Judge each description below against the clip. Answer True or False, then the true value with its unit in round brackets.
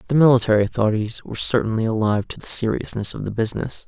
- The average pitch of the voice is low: True (115 Hz)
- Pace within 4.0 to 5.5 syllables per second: False (7.4 syllables/s)